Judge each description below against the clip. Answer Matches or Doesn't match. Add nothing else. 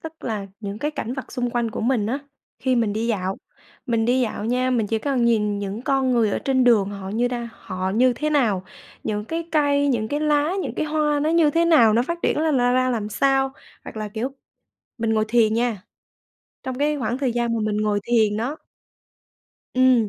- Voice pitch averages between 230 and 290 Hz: Matches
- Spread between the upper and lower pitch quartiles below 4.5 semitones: Matches